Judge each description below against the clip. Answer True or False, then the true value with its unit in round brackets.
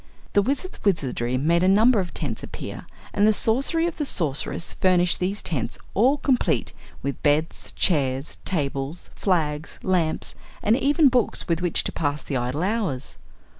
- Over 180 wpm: False (155 wpm)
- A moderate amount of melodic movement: False (6.9 semitones)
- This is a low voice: False (175 Hz)